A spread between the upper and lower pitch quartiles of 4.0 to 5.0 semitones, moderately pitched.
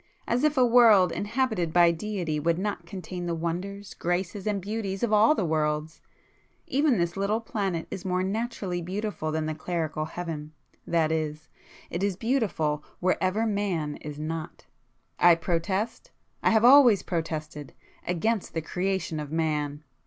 Yes: average, 4.7 semitones; medium, 180 Hz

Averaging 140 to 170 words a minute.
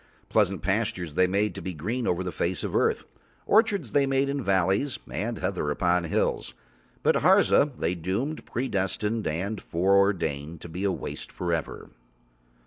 Yes: average, 160 wpm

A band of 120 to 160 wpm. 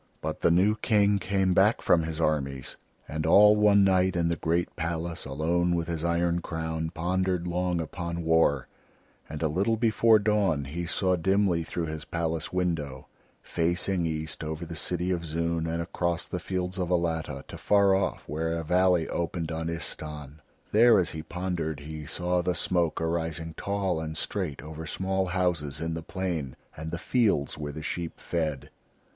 No: average, 175 wpm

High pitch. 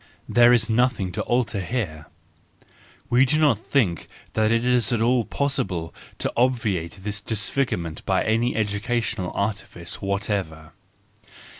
No: low, 110 Hz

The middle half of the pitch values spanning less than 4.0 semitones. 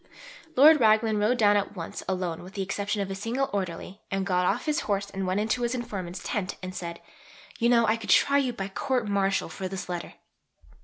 Yes: average, 3.6 semitones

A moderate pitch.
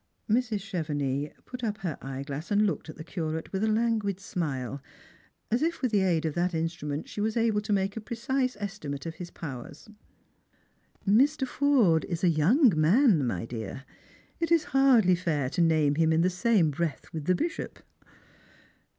Yes: medium, 180 Hz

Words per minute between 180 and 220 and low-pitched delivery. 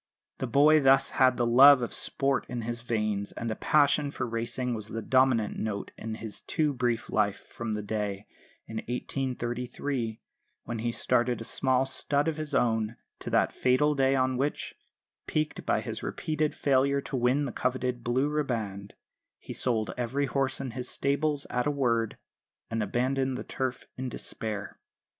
No: average, 170 wpm; low, 125 Hz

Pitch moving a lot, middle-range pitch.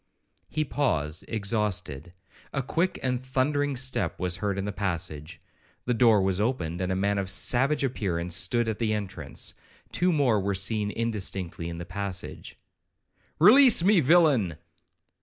No: wide, 5.9 semitones; low, 105 Hz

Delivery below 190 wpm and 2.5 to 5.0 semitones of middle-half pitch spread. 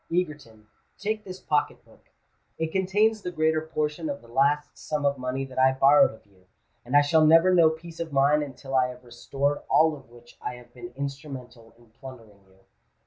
No: average, 195 wpm; average, 4.1 semitones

